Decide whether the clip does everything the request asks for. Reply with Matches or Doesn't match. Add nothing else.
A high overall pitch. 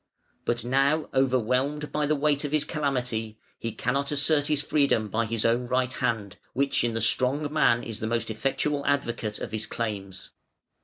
Doesn't match